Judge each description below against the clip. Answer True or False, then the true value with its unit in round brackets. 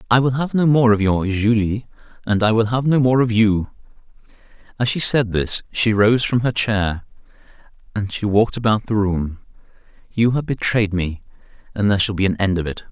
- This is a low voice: True (110 Hz)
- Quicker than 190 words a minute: True (200 wpm)